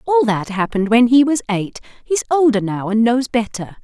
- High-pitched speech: Yes, high, 235 Hz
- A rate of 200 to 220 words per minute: Yes, fast, 205 wpm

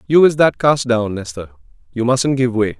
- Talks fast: Yes, fast, 215 wpm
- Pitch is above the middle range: No, low, 130 Hz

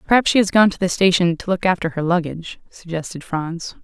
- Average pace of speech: No, fast, 220 wpm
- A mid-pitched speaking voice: Yes, medium, 175 Hz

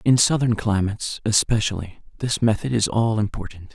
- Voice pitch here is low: Yes, low, 110 Hz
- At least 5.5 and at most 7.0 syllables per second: No, 5.3 syllables/s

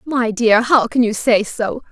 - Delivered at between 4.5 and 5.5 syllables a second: No, 4.0 syllables/s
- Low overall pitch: No, high, 235 Hz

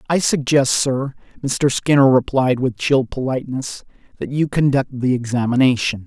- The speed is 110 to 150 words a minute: Yes, average, 140 wpm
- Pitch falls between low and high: No, low, 130 Hz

